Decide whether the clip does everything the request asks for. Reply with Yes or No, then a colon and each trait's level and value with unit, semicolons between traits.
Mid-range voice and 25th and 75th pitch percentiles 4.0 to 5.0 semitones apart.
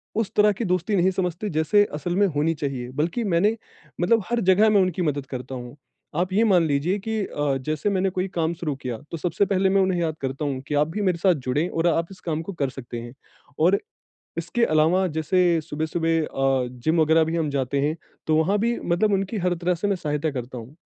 Yes: medium, 165 Hz; average, 4.4 semitones